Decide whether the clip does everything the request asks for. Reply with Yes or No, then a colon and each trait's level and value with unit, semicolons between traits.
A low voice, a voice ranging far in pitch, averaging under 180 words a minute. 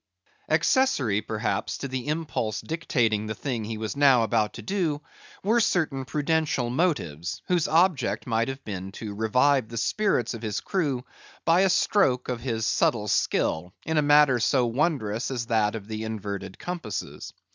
Yes: low, 125 Hz; wide, 5.8 semitones; average, 165 wpm